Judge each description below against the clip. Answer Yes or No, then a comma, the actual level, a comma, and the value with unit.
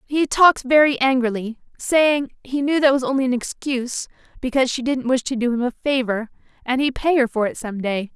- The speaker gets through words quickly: Yes, fast, 215 wpm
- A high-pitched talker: Yes, very high, 260 Hz